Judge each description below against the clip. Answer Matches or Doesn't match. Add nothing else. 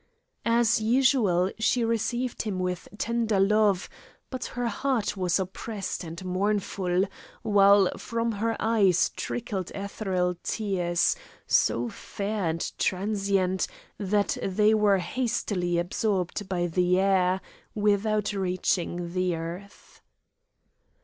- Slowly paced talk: Matches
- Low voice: Doesn't match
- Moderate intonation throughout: Matches